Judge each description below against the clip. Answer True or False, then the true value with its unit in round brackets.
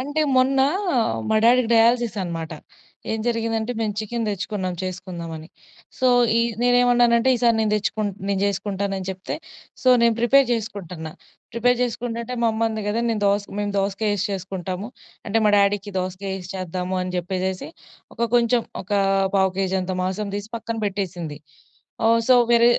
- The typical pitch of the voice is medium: False (205 Hz)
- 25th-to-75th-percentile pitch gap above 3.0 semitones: True (3.7 semitones)